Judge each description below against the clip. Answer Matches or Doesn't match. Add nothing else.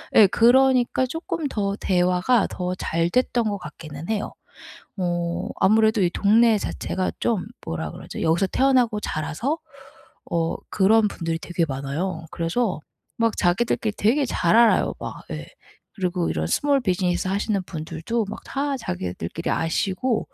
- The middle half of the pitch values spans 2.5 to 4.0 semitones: Doesn't match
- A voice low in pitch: Doesn't match